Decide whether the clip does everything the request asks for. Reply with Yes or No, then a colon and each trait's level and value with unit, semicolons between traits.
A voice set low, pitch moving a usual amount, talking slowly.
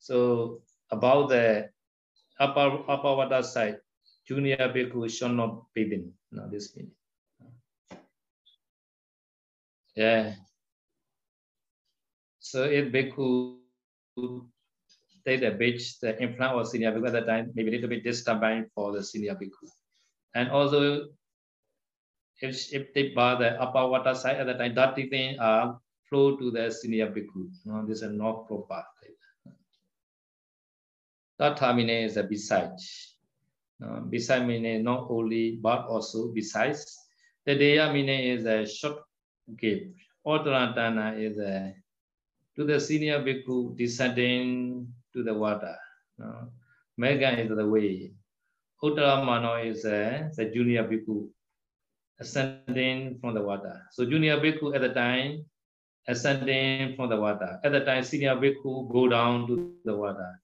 Yes: low, 125 Hz; average, 3.2 semitones; slow, 130 wpm